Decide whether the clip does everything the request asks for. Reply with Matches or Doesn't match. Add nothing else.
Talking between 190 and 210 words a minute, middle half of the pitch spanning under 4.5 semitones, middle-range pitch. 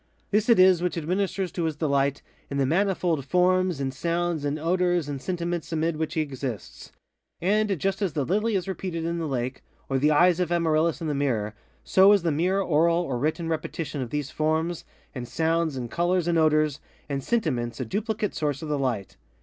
Matches